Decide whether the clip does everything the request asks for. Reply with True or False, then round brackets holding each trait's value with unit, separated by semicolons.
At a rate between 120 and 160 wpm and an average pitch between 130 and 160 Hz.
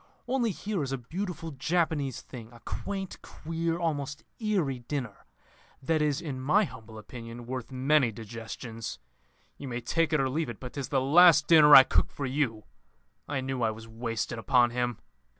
False (175 wpm; 135 Hz)